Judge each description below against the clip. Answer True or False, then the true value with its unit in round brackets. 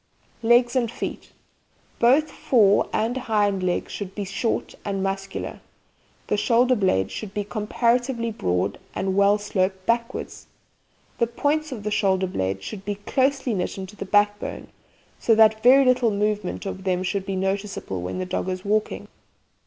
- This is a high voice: True (205 Hz)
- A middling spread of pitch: True (3.5 semitones)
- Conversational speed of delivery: True (160 wpm)